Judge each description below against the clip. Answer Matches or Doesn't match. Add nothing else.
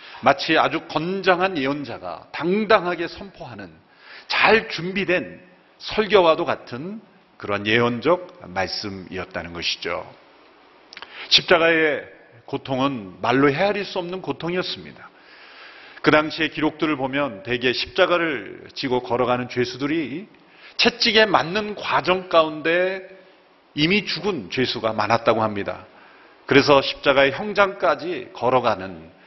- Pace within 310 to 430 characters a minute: Doesn't match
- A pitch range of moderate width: Doesn't match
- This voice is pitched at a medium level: Matches